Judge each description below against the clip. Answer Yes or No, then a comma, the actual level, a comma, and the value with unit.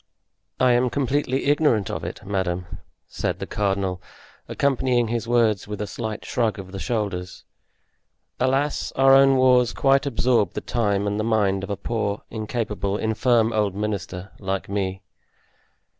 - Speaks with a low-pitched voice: Yes, low, 110 Hz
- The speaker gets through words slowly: No, average, 150 wpm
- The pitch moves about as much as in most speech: Yes, average, 4.0 semitones